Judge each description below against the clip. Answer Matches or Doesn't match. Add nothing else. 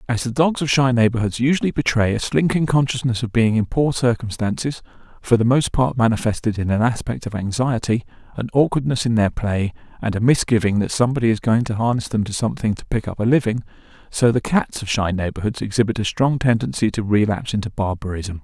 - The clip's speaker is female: Doesn't match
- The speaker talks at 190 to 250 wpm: Matches